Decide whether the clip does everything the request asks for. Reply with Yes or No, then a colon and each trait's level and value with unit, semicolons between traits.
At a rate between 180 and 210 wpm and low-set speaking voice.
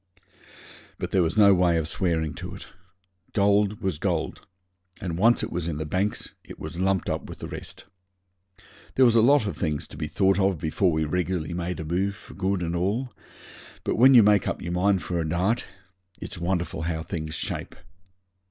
Yes: average, 200 wpm; very low, 90 Hz